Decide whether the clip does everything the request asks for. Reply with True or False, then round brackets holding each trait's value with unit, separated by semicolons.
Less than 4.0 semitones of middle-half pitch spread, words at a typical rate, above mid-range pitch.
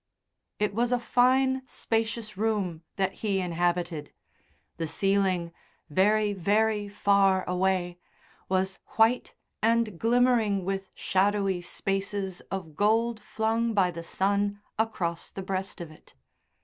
False (3.0 semitones; 120 wpm; 200 Hz)